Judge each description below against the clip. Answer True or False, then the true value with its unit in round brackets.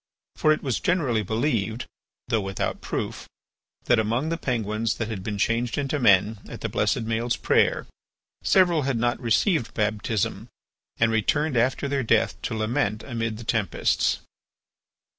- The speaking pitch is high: False (115 Hz)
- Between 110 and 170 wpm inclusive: True (150 wpm)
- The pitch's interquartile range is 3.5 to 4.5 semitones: True (3.8 semitones)